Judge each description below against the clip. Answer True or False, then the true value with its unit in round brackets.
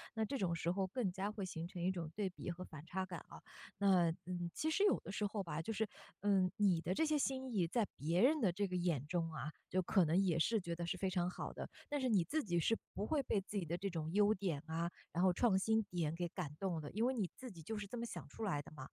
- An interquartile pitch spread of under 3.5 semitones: False (3.8 semitones)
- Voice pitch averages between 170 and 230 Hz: True (185 Hz)